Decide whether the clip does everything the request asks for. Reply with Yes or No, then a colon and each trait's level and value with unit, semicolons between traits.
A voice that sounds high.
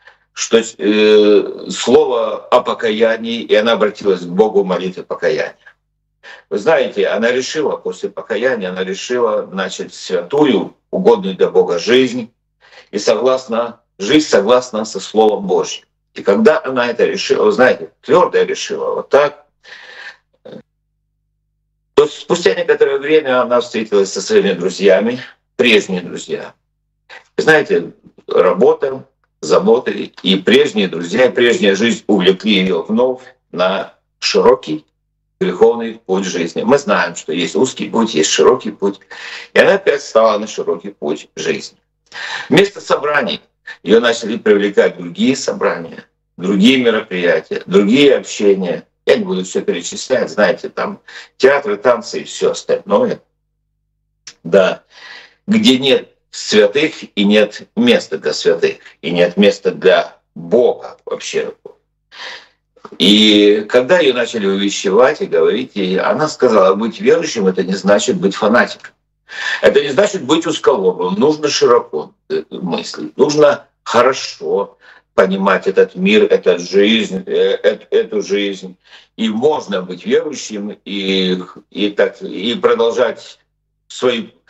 Yes: high, 225 Hz